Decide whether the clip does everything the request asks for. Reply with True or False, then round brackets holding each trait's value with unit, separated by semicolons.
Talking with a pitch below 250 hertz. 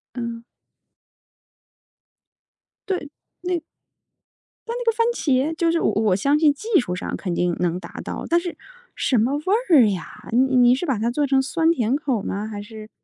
False (260 Hz)